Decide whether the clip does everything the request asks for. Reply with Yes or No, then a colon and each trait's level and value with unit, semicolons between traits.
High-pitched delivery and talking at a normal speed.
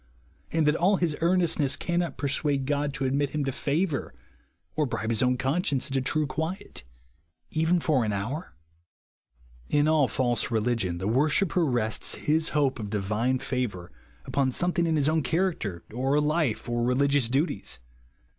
No: medium, 140 Hz; average, 155 wpm